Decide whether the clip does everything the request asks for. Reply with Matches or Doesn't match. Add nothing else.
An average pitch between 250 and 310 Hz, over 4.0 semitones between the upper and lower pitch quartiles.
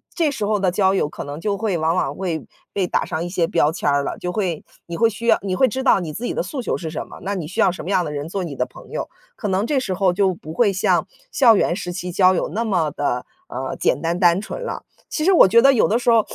Doesn't match